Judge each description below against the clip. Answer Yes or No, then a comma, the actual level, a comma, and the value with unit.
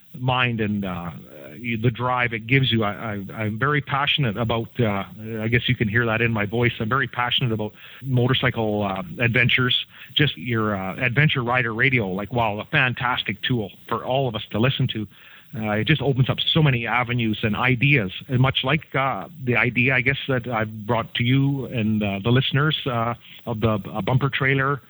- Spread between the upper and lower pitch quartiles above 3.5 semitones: No, average, 3.2 semitones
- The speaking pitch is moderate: No, low, 120 Hz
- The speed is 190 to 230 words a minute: Yes, average, 200 wpm